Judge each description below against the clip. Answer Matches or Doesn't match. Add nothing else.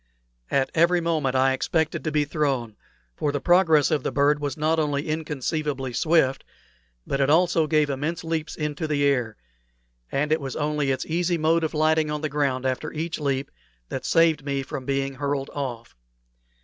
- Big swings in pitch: Doesn't match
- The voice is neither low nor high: Matches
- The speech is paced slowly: Doesn't match